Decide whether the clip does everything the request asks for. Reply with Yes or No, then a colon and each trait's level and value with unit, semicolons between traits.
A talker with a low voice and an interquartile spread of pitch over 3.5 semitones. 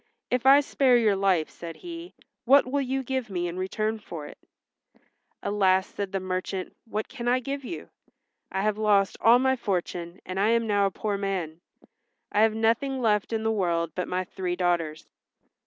No: high, 205 Hz; average, 4.6 semitones